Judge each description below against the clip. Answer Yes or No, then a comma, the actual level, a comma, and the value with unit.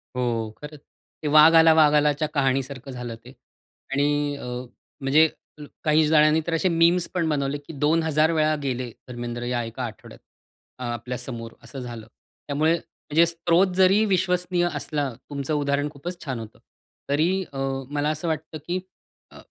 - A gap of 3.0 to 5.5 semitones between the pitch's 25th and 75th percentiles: Yes, average, 3.4 semitones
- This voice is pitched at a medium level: Yes, medium, 150 Hz